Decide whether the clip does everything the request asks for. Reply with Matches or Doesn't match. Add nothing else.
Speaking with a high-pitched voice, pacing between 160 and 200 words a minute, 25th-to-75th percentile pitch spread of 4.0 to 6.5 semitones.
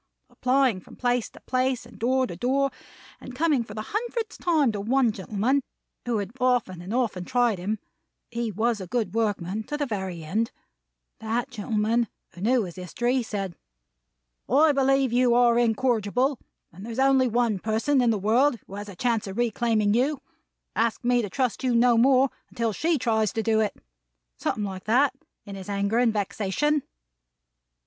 Doesn't match